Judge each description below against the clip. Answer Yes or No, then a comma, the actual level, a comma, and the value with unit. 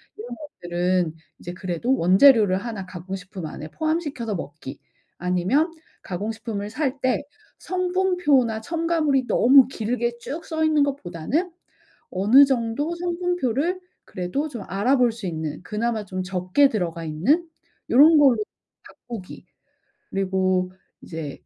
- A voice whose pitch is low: No, high, 230 Hz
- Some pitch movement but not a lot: No, wide, 7.7 semitones